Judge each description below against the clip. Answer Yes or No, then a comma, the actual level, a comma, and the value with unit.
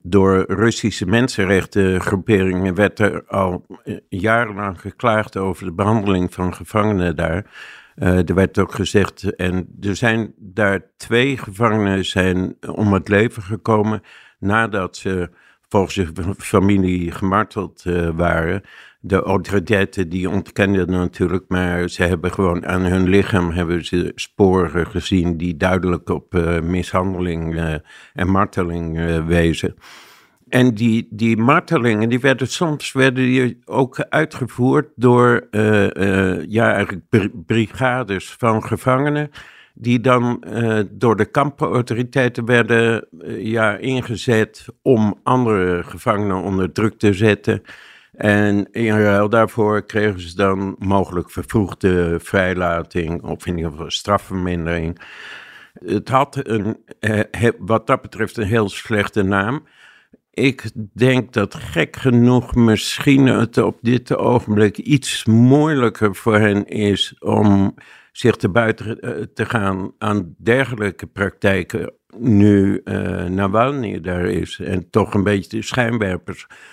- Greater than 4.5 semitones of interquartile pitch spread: No, average, 3.7 semitones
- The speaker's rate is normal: No, slow, 125 wpm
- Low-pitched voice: Yes, low, 100 Hz